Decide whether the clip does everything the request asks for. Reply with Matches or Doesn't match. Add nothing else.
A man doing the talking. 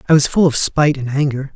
Matches